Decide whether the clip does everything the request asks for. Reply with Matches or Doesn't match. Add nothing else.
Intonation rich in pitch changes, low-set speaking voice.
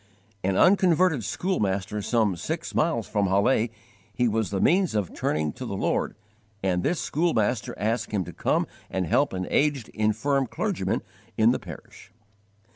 Matches